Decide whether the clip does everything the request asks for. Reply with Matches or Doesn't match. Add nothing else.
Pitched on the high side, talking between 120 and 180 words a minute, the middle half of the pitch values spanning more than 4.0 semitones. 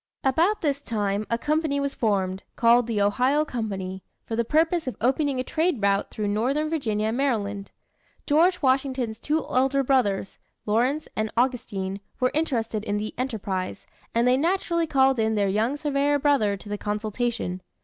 Matches